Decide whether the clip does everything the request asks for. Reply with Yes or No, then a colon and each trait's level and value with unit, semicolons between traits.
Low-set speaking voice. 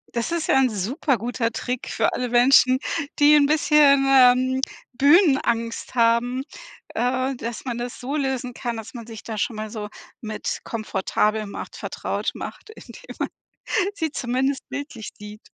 No: very high, 250 Hz